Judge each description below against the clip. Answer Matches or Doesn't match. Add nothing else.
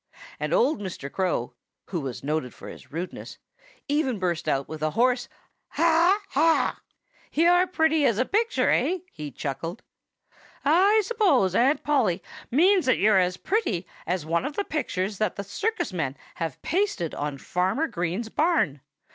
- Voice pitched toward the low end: Doesn't match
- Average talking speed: Matches